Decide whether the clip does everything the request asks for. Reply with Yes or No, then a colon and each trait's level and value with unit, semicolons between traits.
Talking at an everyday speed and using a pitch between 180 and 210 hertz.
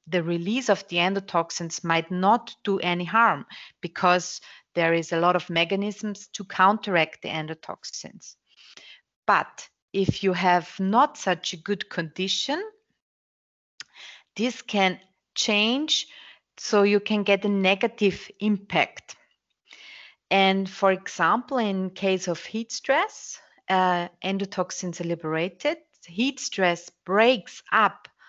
No: slow, 120 wpm; high, 190 Hz